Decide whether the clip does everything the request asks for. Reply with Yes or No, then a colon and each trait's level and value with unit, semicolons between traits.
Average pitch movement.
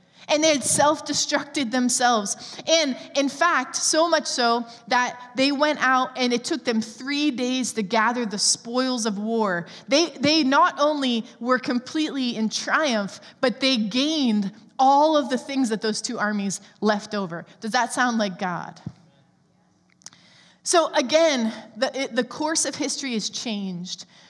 Yes: average, 4.7 semitones